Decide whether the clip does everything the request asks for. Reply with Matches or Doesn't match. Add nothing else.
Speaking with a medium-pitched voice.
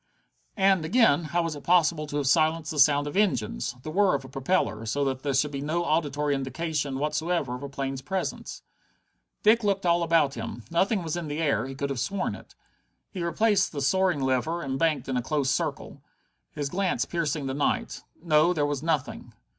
Matches